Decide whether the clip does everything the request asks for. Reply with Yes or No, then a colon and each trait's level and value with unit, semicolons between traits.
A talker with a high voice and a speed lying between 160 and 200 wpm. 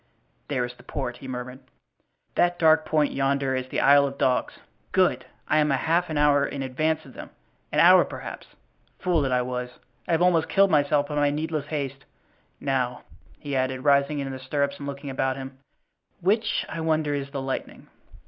No: medium, 140 Hz; average, 190 wpm